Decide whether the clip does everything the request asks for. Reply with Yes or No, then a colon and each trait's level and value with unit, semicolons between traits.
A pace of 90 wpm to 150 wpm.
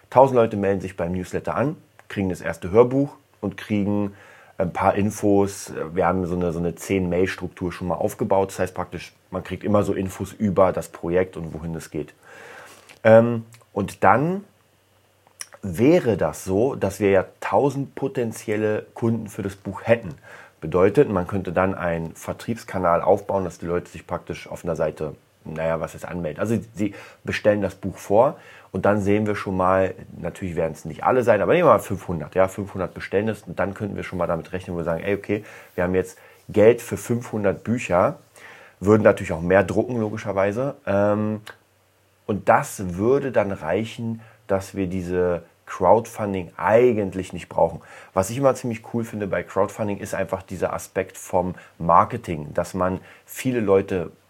No: average, 175 wpm